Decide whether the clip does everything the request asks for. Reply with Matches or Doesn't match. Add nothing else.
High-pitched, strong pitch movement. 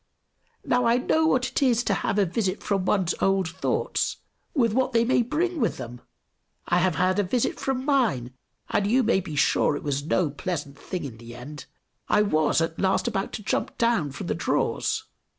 Matches